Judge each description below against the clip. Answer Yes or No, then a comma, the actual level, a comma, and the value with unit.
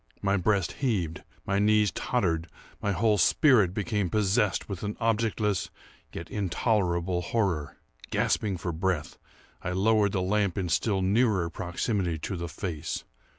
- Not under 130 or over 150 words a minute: Yes, average, 140 wpm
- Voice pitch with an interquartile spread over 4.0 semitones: No, average, 3.4 semitones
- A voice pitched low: Yes, very low, 95 Hz